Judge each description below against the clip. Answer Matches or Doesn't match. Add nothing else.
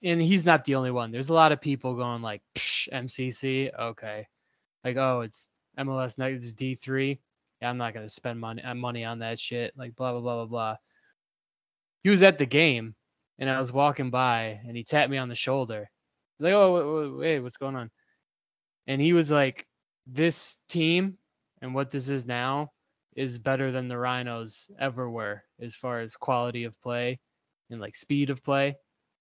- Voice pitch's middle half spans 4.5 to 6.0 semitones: Doesn't match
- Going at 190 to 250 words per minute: Matches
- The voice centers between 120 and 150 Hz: Matches